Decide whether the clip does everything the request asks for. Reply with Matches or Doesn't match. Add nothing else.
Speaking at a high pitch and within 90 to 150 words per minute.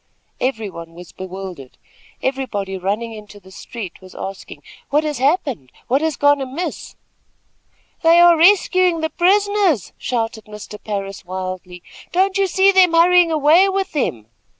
Matches